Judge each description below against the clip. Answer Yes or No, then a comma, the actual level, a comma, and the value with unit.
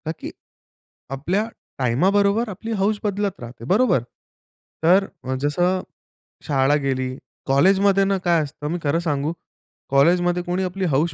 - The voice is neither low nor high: Yes, medium, 175 Hz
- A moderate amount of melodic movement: No, wide, 5.7 semitones